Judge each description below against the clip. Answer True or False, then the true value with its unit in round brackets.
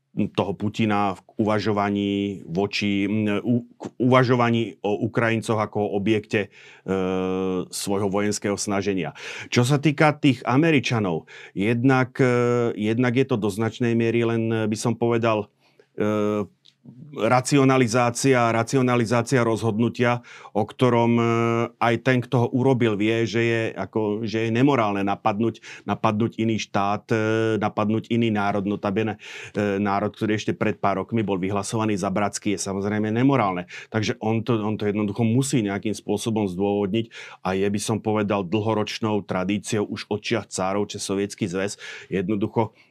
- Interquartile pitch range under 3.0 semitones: True (2.4 semitones)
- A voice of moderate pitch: False (110 Hz)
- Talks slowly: False (135 wpm)